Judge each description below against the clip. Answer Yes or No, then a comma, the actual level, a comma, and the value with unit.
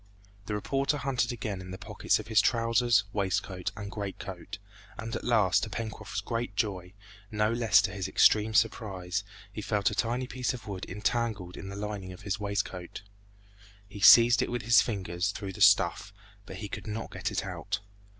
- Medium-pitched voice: No, low, 105 Hz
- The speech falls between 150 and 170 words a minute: No, average, 190 wpm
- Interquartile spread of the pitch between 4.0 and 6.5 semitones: No, average, 3.0 semitones